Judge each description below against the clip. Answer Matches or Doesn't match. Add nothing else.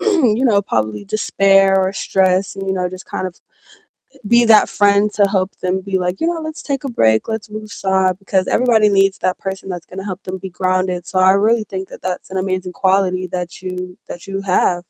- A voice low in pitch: Doesn't match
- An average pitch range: Doesn't match